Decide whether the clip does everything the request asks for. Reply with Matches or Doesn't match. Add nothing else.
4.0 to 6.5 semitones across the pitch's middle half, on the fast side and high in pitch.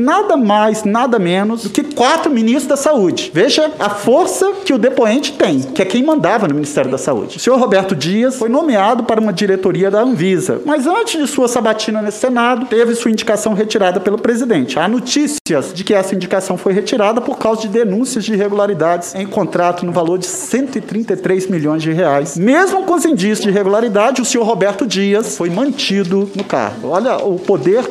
Matches